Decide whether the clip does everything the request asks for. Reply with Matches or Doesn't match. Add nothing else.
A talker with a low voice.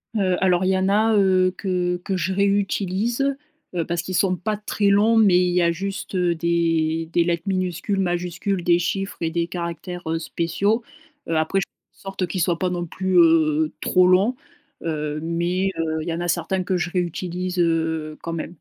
Doesn't match